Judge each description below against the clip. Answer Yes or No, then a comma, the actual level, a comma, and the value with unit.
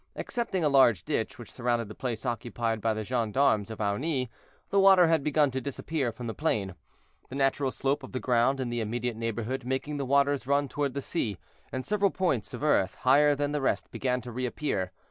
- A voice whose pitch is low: Yes, low, 130 Hz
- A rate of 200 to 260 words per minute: Yes, fast, 205 wpm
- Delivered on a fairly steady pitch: No, average, 3.6 semitones